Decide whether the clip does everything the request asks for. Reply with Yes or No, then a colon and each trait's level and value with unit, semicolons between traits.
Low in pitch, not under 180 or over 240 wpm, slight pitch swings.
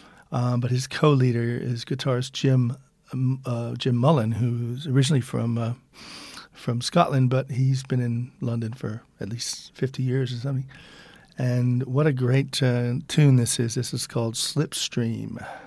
No: low, 130 Hz; average, 155 wpm; narrow, 2.1 semitones